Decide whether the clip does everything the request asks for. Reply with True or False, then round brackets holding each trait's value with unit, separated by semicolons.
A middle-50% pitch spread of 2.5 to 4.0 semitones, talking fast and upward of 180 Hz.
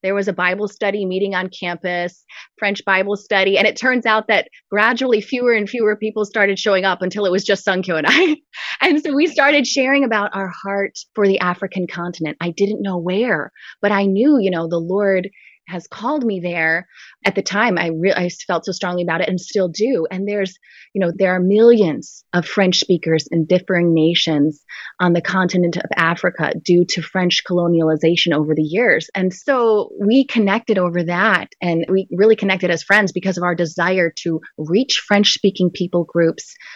False (2.9 semitones; 195 wpm; 190 Hz)